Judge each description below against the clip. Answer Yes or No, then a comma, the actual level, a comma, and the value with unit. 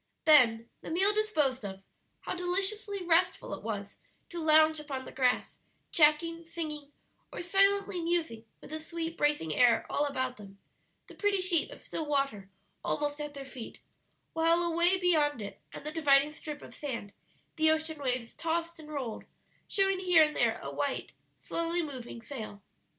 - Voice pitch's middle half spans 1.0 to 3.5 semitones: No, average, 4.5 semitones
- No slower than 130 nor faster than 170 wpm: Yes, average, 165 wpm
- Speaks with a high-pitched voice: Yes, very high, 310 Hz